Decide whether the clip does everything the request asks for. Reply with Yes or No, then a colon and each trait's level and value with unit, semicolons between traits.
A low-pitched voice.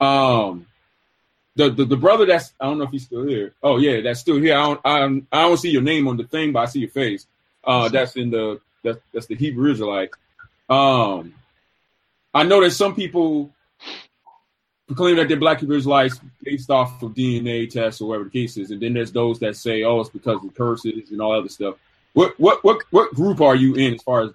Yes: low, 130 Hz